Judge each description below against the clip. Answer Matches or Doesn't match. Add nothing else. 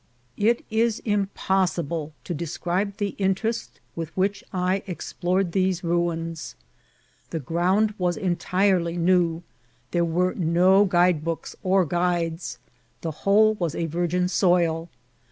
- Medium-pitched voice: Matches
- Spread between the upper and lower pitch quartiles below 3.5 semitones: Matches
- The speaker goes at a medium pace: Doesn't match